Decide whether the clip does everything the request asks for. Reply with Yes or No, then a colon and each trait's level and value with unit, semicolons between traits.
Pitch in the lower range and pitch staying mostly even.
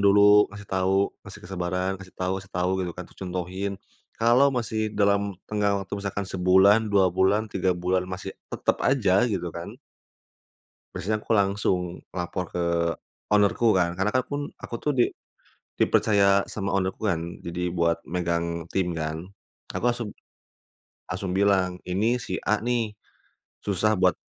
Yes: very low, 95 Hz; narrow, 2.3 semitones